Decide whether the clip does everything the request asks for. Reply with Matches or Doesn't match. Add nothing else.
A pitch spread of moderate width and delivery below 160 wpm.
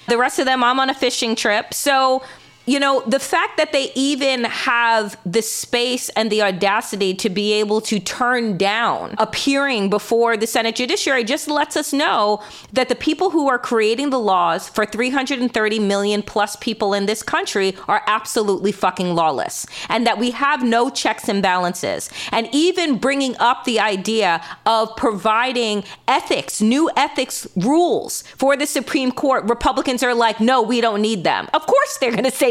Doesn't match